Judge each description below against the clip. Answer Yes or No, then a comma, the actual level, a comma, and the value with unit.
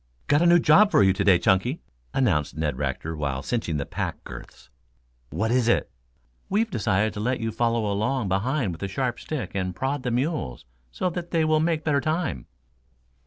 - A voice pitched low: Yes, low, 115 Hz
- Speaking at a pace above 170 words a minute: Yes, average, 190 wpm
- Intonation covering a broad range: Yes, wide, 8.3 semitones